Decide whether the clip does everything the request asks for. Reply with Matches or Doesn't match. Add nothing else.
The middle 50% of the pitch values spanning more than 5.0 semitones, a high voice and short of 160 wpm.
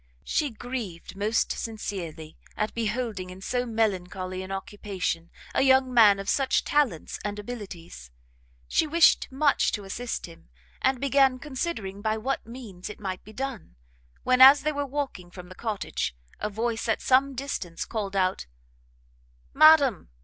Matches